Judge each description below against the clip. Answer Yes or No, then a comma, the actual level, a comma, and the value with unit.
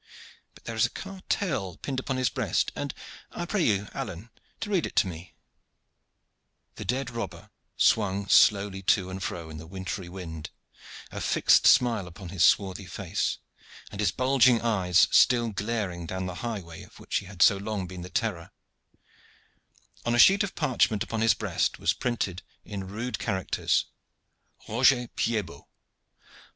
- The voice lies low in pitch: Yes, low, 100 Hz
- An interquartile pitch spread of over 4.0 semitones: Yes, average, 4.5 semitones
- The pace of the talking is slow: No, average, 165 wpm